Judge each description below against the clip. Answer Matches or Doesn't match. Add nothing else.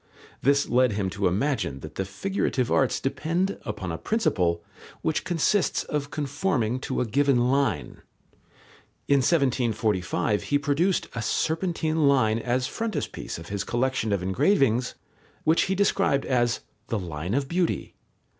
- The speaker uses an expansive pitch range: Matches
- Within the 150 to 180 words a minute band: Doesn't match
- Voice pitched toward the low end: Matches